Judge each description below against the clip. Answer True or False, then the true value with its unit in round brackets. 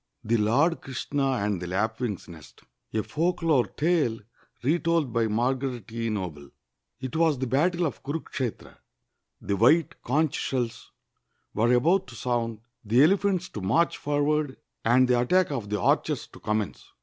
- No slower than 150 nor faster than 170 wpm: True (155 wpm)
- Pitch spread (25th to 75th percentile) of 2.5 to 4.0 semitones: False (5.6 semitones)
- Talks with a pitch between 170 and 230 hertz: False (125 Hz)